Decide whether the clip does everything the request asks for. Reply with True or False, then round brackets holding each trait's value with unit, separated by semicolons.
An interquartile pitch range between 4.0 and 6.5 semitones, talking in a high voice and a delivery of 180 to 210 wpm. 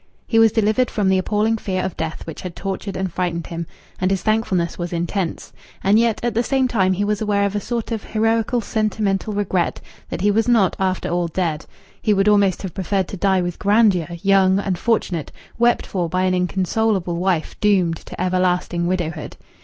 False (3.1 semitones; 195 Hz; 195 wpm)